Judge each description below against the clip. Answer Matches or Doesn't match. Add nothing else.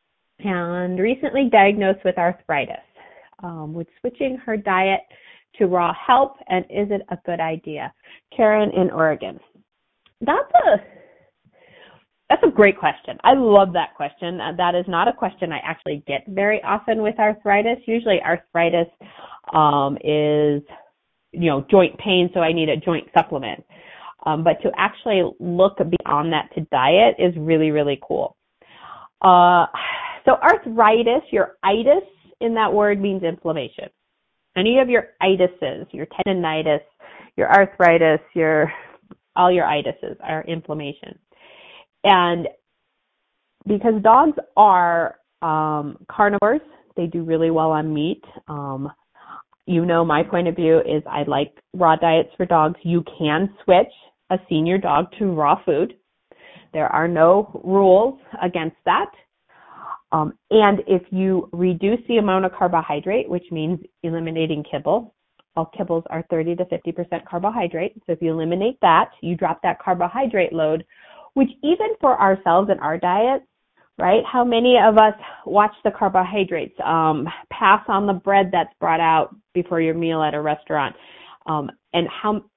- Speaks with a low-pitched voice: Doesn't match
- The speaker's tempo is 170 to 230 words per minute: Doesn't match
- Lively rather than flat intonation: Doesn't match